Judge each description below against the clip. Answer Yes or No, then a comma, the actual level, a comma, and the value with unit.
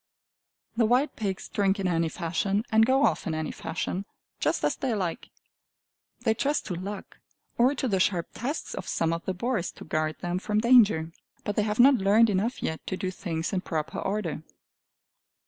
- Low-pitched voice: No, high, 195 Hz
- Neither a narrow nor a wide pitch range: Yes, average, 4.7 semitones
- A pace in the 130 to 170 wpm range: No, average, 190 wpm